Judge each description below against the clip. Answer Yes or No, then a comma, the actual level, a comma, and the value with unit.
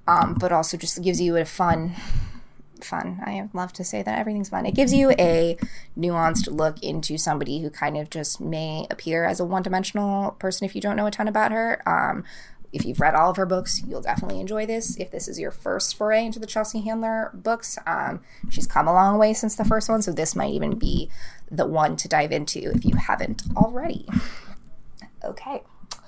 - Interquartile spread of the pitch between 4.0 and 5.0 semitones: Yes, average, 4.4 semitones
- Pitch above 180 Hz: Yes, high, 190 Hz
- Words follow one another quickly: Yes, fast, 210 wpm